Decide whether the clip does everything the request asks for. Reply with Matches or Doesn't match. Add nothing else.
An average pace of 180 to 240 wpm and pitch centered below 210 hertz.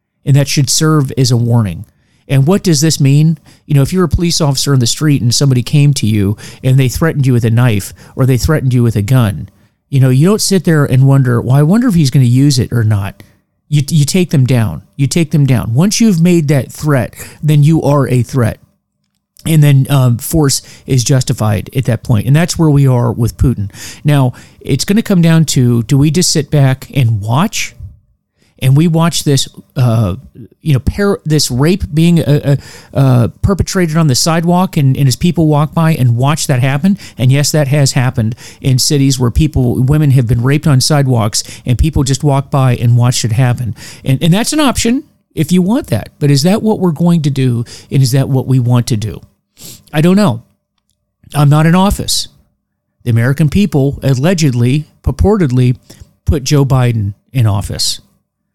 Matches